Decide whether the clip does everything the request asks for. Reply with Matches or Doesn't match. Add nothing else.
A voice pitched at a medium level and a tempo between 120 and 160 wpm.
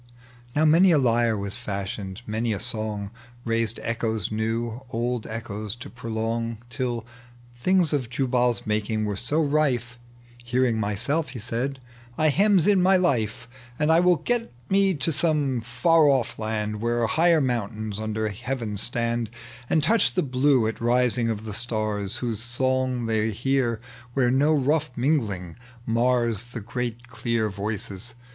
Doesn't match